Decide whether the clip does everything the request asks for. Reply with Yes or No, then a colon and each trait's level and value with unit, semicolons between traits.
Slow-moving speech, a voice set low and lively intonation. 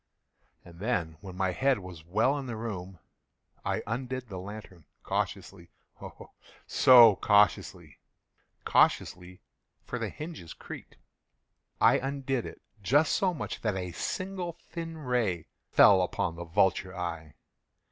Yes: slow, 120 wpm; low, 105 Hz; wide, 6.4 semitones